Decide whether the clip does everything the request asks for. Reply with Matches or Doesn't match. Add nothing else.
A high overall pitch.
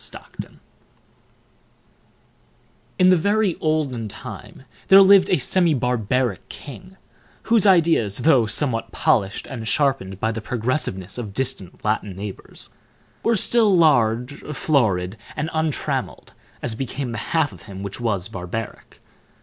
Doesn't match